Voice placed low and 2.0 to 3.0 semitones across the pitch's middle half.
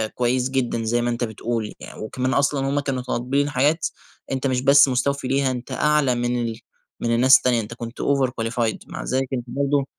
Yes: low, 130 Hz; narrow, 2.4 semitones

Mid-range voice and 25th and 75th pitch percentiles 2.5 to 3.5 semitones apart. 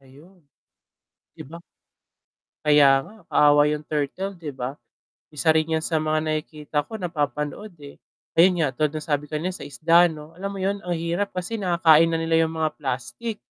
Yes: medium, 155 Hz; average, 3.0 semitones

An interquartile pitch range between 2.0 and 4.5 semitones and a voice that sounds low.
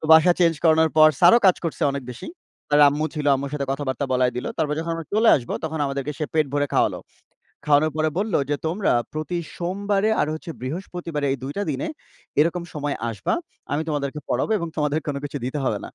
No: average, 2.9 semitones; medium, 150 Hz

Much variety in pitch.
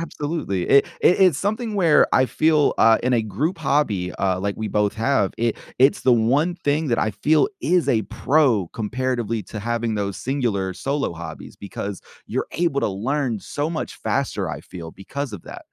Yes: wide, 6.3 semitones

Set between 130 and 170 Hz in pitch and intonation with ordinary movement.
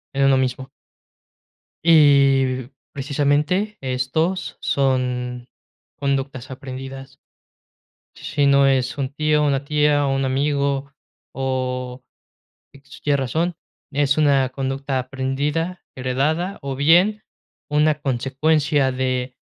No: low, 135 Hz; narrow, 2.1 semitones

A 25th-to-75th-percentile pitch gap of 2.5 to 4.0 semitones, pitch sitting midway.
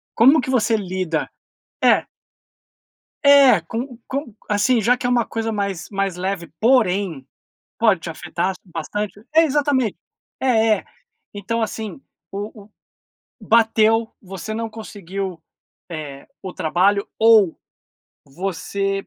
No: average, 3.5 semitones; high, 205 Hz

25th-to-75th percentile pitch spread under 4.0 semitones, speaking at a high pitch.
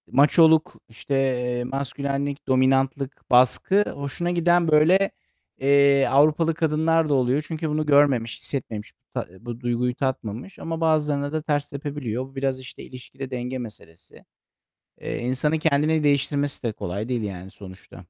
No: average, 3.4 semitones; medium, 140 Hz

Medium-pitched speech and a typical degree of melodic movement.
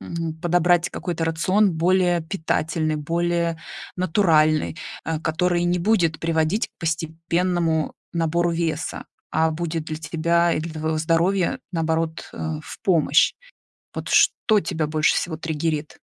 No: medium, 165 Hz; narrow, 1.6 semitones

